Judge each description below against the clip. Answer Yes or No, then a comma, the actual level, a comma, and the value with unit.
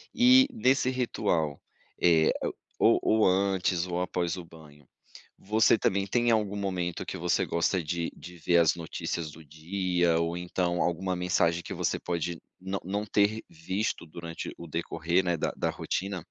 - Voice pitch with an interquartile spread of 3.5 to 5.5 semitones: No, average, 2.8 semitones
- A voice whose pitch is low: Yes, very low, 90 Hz